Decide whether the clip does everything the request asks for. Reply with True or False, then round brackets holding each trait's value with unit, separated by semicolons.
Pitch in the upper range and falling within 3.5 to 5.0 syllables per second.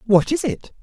True (235 Hz; 4.7 syllables/s)